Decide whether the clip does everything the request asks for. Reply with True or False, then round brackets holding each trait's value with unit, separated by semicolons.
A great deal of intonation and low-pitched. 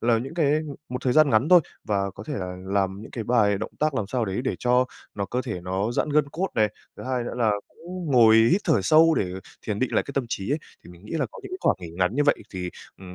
True (6.7 semitones; 120 Hz)